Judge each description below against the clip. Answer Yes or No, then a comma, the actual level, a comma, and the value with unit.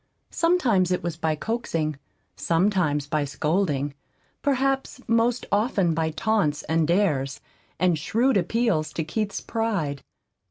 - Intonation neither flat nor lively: No, wide, 6.5 semitones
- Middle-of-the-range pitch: Yes, medium, 180 Hz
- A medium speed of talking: No, slow, 120 wpm